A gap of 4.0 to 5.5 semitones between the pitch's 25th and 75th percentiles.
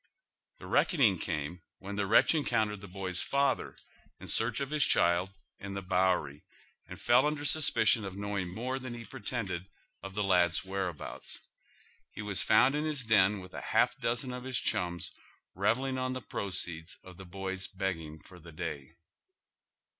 Yes: average, 5.2 semitones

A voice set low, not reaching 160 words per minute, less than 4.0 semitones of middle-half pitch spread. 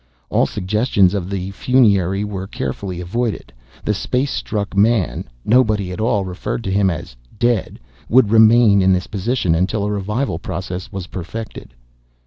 Yes: low, 100 Hz; average, 150 wpm; average, 3.2 semitones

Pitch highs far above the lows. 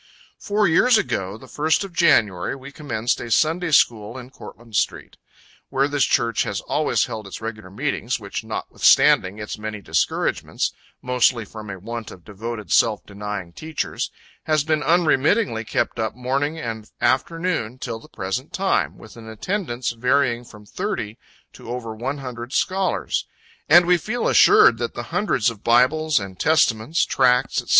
Yes: wide, 5.9 semitones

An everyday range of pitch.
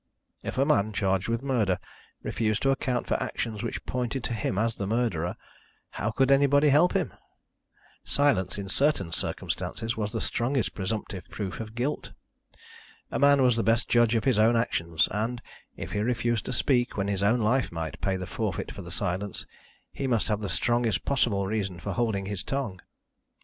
Yes: average, 3.9 semitones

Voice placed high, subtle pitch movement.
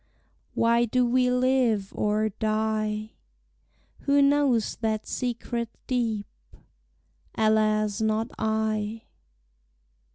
Yes: high, 220 Hz; narrow, 2.2 semitones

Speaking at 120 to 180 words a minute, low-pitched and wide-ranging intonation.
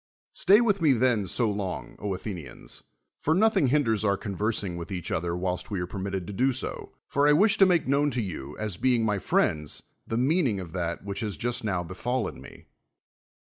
No: average, 200 wpm; low, 105 Hz; wide, 6.2 semitones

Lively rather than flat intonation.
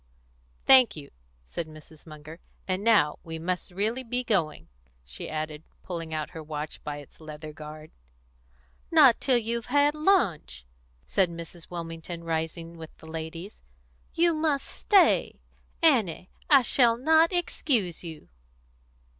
Yes: wide, 7.7 semitones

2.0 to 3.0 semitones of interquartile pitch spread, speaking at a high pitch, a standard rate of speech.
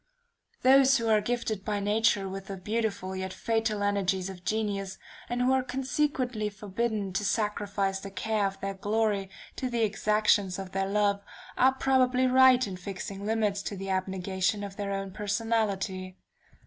Yes: narrow, 2.6 semitones; high, 205 Hz; average, 160 wpm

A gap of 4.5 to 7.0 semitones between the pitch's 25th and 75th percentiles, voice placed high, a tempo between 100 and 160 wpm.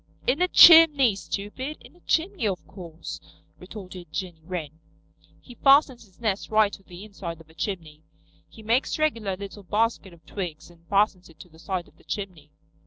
No: average, 4.8 semitones; high, 195 Hz; average, 185 wpm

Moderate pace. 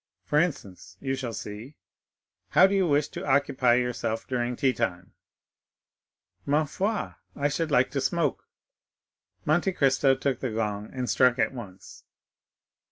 Yes: average, 145 wpm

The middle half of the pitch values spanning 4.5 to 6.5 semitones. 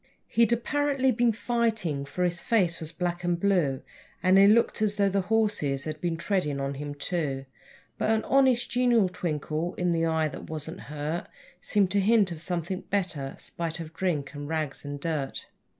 Yes: average, 5.2 semitones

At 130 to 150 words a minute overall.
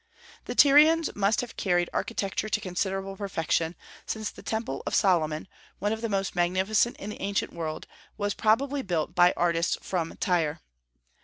No: average, 160 wpm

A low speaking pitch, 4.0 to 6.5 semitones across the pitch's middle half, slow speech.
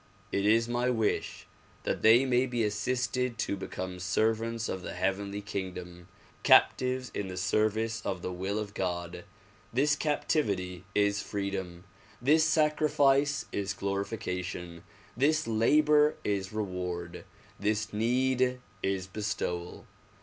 Yes: low, 105 Hz; average, 5.0 semitones; slow, 120 wpm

